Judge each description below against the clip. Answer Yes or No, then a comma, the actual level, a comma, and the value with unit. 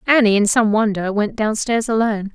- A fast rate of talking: No, average, 180 wpm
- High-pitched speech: Yes, high, 215 Hz